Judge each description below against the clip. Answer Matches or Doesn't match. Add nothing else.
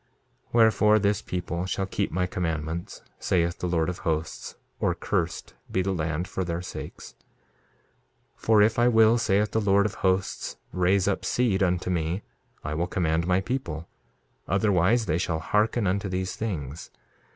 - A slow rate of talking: Doesn't match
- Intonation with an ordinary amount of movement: Matches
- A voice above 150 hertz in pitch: Doesn't match